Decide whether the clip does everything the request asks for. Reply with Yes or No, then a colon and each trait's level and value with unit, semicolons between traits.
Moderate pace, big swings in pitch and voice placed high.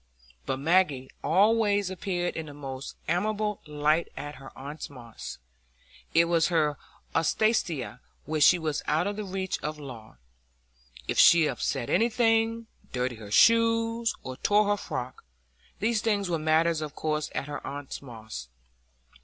No: average, 145 wpm; wide, 7.2 semitones; medium, 155 Hz